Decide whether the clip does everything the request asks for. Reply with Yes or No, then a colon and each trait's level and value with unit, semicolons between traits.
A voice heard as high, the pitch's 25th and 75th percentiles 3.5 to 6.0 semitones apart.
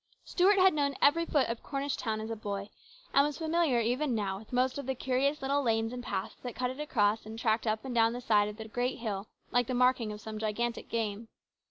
Yes: high, 240 Hz; average, 3.8 semitones